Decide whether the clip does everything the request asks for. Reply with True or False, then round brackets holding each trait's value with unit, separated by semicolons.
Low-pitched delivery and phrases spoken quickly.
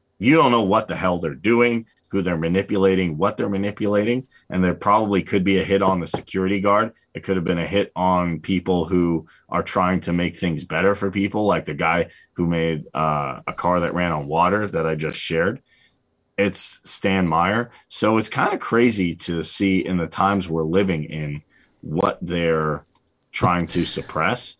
False (90 Hz; 195 wpm)